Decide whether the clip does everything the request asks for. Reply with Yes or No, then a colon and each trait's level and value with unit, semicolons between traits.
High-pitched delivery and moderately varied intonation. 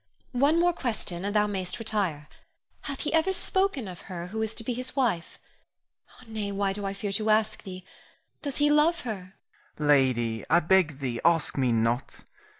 No: high, 200 Hz; wide, 6.4 semitones